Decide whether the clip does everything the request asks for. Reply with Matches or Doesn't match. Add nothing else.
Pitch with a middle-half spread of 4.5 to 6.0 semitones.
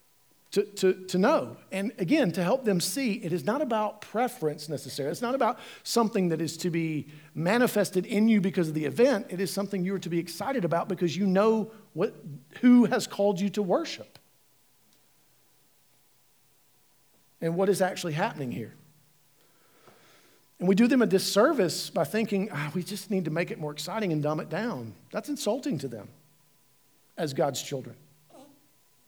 Matches